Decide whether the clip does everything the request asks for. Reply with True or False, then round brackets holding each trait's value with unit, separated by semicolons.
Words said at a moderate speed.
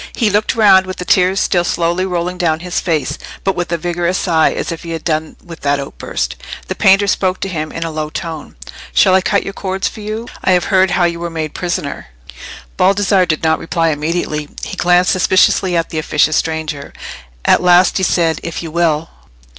False (210 wpm)